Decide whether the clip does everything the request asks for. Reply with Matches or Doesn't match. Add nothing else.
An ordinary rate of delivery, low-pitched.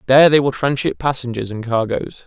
Matches